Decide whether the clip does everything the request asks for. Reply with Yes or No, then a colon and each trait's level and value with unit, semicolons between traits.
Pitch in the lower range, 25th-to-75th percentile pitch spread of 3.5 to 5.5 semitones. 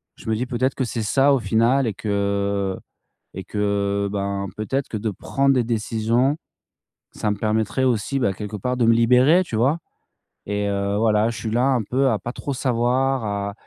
Yes: low, 115 Hz; average, 3.8 semitones